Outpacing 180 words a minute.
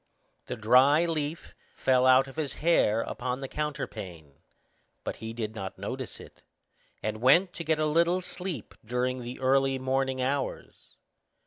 No: average, 150 wpm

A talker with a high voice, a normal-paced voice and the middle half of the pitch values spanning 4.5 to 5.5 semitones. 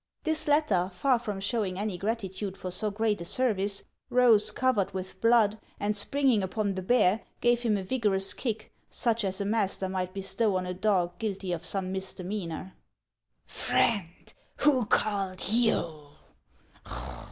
No: high, 205 Hz; average, 150 wpm; average, 3.4 semitones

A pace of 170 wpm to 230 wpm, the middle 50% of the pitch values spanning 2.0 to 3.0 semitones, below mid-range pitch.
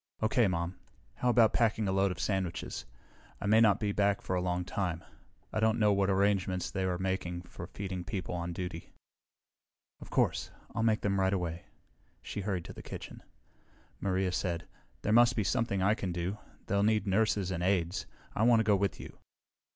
Yes: average, 195 wpm; average, 2.7 semitones; very low, 95 Hz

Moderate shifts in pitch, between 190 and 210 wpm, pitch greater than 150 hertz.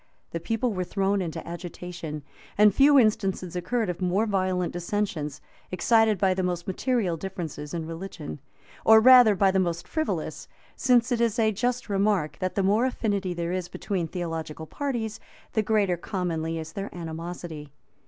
No: average, 4.1 semitones; average, 165 wpm; medium, 185 Hz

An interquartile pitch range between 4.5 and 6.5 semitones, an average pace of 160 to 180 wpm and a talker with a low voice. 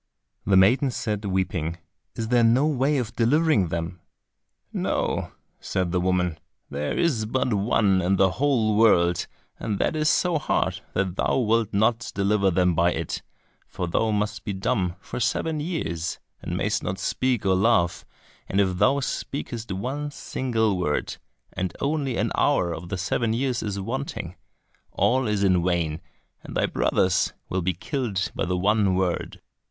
Yes: average, 5.0 semitones; average, 165 wpm; low, 100 Hz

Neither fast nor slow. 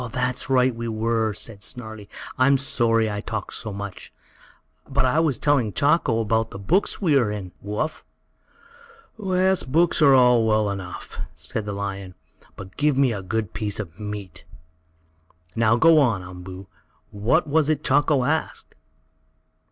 Yes: average, 155 wpm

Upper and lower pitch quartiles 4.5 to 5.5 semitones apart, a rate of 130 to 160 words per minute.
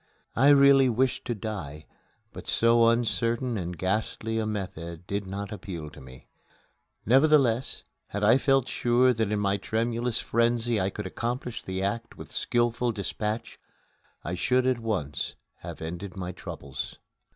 No: average, 4.0 semitones; average, 150 wpm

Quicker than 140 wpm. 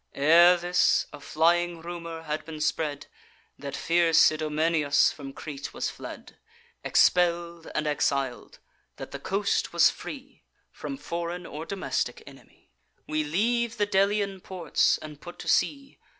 No: slow, 135 wpm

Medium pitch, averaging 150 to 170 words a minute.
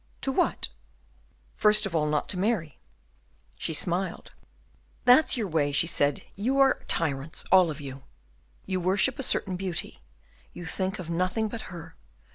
Yes: medium, 180 Hz; average, 155 wpm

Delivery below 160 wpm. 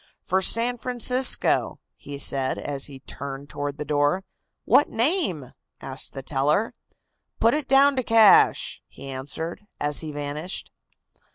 Yes: slow, 135 wpm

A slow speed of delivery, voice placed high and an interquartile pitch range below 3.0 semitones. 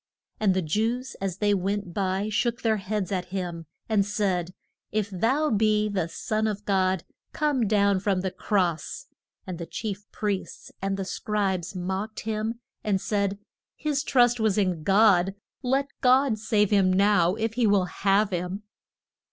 No: average, 160 wpm; high, 205 Hz; narrow, 2.6 semitones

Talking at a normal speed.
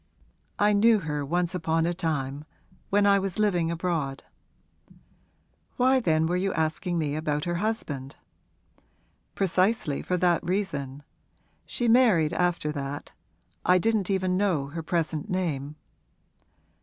No: slow, 130 wpm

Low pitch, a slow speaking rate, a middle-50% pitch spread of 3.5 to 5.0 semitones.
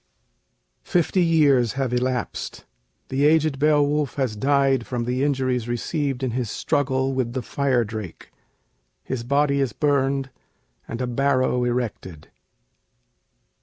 No: low, 130 Hz; slow, 125 wpm; narrow, 2.5 semitones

